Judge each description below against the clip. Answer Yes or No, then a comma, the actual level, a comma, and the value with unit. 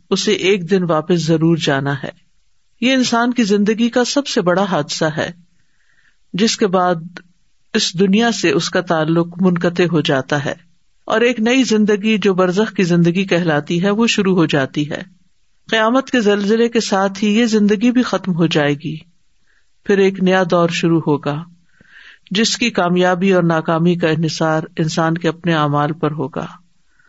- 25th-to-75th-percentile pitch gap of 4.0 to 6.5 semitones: Yes, average, 4.5 semitones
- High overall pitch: No, medium, 180 Hz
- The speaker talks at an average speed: Yes, average, 170 wpm